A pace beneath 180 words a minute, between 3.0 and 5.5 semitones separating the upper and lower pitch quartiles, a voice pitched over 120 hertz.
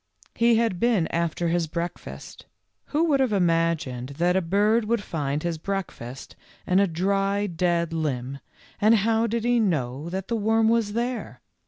Yes: average, 170 wpm; average, 5.2 semitones; high, 190 Hz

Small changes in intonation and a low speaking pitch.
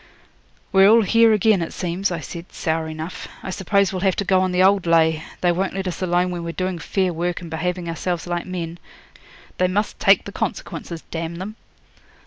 No: narrow, 2.2 semitones; medium, 180 Hz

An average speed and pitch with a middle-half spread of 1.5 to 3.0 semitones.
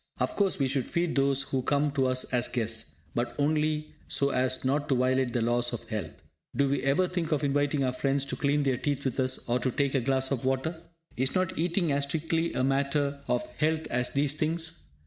No: fast, 225 wpm; average, 2.7 semitones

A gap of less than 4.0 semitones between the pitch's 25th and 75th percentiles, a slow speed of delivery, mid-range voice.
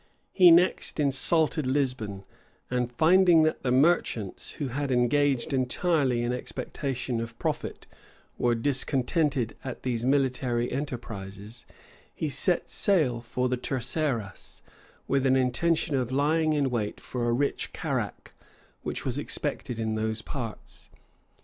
No: average, 3.5 semitones; slow, 130 wpm; low, 130 Hz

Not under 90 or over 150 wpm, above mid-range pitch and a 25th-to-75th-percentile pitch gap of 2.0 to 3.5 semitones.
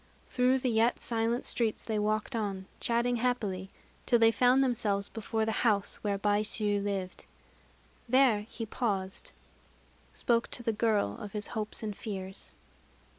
Yes: average, 145 wpm; high, 220 Hz; narrow, 2.6 semitones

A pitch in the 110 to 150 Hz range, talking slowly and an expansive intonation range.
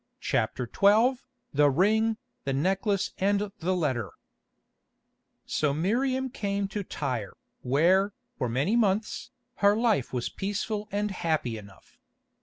No: high, 195 Hz; slow, 120 wpm; wide, 7.0 semitones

